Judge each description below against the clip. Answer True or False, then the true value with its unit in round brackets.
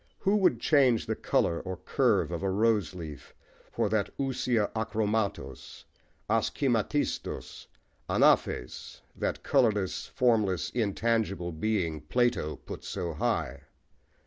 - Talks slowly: True (110 wpm)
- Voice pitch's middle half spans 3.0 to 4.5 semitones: False (5.0 semitones)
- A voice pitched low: True (105 Hz)